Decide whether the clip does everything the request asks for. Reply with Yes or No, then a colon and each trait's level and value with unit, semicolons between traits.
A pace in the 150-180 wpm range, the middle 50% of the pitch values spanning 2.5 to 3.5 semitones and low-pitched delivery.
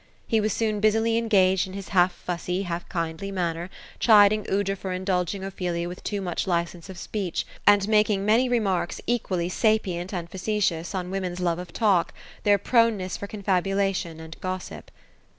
No: average, 170 wpm; average, 2.8 semitones; high, 190 Hz